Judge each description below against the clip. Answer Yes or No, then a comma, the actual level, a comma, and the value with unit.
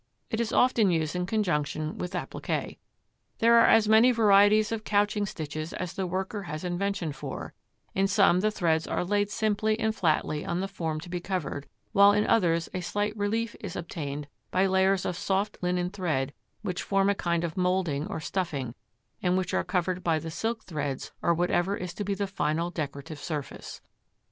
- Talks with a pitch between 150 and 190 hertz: Yes, medium, 185 Hz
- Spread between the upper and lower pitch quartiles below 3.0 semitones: No, average, 3.7 semitones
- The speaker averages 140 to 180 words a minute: No, average, 190 wpm